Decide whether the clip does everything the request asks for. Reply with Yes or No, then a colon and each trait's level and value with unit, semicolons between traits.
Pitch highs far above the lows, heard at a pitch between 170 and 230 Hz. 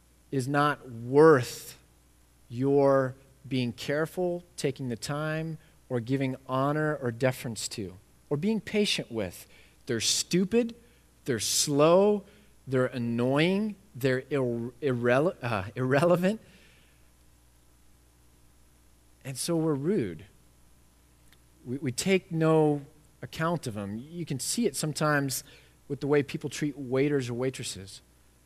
No: wide, 6.4 semitones; low, 135 Hz